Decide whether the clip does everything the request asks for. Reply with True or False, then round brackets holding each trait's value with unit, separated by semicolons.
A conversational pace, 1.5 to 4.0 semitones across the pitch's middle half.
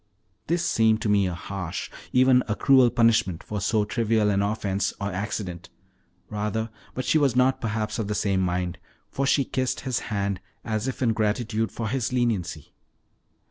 True (175 wpm; 3.4 semitones)